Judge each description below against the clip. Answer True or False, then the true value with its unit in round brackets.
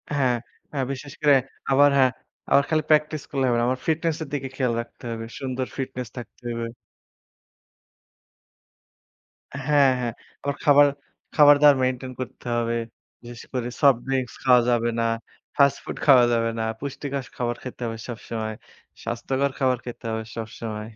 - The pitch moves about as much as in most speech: True (3.0 semitones)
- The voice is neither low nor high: False (130 Hz)